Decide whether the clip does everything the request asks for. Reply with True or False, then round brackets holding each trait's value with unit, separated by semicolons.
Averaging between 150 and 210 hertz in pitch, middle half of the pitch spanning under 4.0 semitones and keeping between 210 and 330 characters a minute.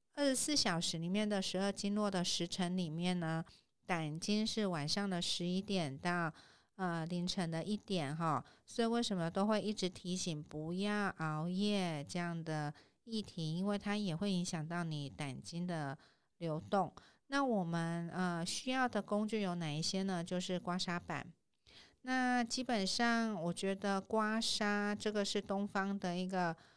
True (185 Hz; 3.5 semitones; 240 characters per minute)